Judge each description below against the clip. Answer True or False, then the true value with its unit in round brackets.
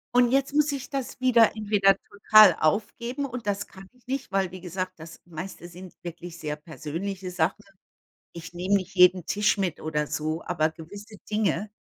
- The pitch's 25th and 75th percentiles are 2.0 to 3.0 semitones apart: False (3.9 semitones)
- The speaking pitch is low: False (190 Hz)